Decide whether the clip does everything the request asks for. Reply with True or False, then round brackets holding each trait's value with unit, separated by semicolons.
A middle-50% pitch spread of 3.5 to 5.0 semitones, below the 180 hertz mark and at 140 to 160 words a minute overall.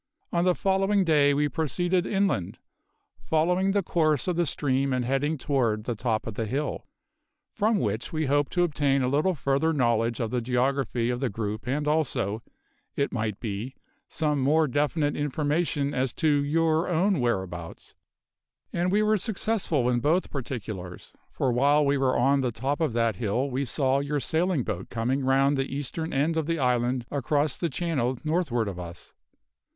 False (4.6 semitones; 140 Hz; 175 wpm)